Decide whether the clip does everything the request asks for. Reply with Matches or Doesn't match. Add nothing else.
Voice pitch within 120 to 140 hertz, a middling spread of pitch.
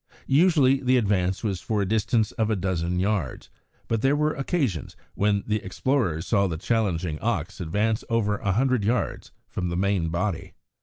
Doesn't match